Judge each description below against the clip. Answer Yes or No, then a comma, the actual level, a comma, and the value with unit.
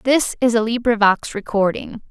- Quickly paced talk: No, average, 140 wpm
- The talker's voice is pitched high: Yes, high, 225 Hz